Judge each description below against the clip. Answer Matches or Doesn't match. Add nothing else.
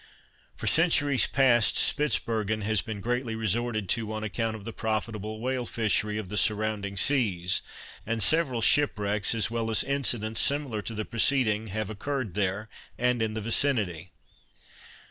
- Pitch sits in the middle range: Doesn't match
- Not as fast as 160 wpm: Matches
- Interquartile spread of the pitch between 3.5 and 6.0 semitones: Doesn't match